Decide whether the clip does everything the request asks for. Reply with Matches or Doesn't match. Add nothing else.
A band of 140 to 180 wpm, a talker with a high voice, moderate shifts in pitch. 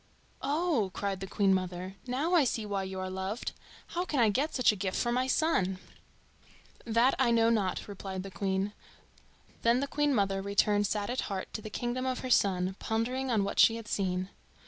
Doesn't match